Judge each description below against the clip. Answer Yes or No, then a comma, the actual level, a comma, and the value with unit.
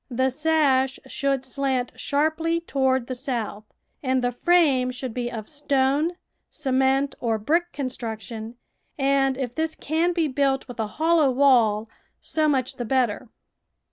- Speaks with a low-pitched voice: No, very high, 265 Hz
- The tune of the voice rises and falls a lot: No, average, 2.9 semitones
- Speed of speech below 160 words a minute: Yes, average, 140 wpm